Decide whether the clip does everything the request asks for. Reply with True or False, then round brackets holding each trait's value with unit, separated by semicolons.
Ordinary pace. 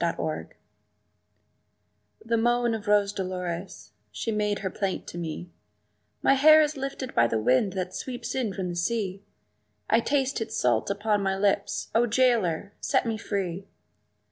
True (160 wpm)